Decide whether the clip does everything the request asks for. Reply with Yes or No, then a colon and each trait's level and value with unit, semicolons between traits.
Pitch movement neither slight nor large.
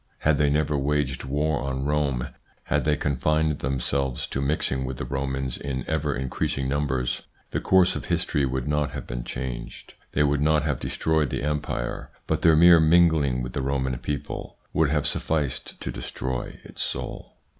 No: narrow, 2.3 semitones